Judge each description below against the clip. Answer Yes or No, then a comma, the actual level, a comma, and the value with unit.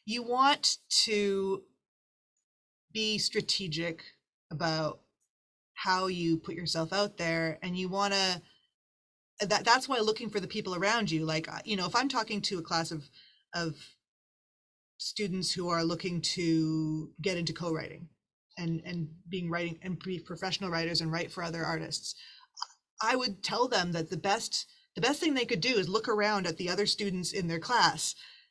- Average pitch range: Yes, average, 4.1 semitones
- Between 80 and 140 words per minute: No, average, 170 wpm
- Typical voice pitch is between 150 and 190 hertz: Yes, medium, 185 Hz